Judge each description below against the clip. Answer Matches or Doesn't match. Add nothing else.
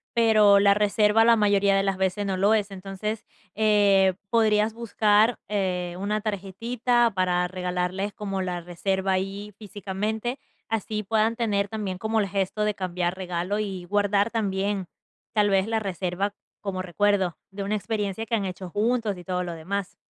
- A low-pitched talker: Doesn't match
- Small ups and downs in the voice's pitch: Matches